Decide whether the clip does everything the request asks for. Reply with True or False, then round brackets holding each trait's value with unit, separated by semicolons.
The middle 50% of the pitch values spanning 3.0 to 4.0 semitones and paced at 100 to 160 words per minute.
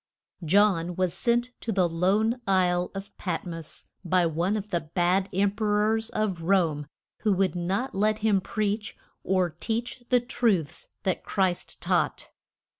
True (3.4 semitones; 155 wpm)